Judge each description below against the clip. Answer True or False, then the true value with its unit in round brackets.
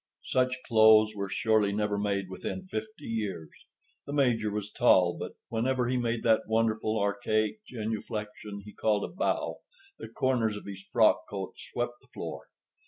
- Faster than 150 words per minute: True (160 wpm)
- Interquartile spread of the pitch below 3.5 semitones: True (2.7 semitones)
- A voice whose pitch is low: True (110 Hz)